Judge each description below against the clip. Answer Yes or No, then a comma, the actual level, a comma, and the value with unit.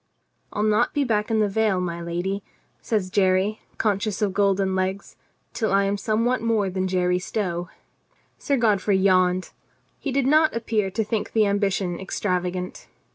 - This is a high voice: Yes, high, 200 Hz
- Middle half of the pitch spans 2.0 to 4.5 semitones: Yes, average, 2.7 semitones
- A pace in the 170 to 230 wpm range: No, average, 160 wpm